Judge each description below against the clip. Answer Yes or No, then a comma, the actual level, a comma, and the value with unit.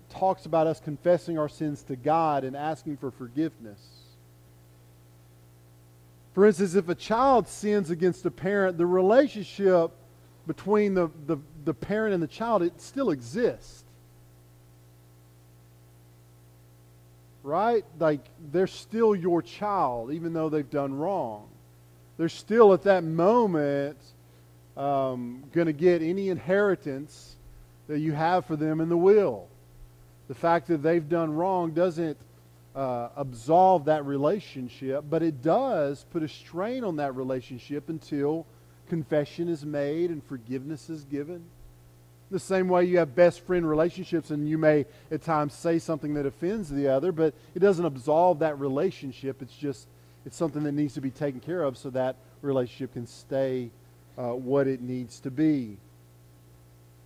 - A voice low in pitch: No, medium, 145 Hz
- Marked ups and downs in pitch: Yes, wide, 7.9 semitones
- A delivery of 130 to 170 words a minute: Yes, average, 145 wpm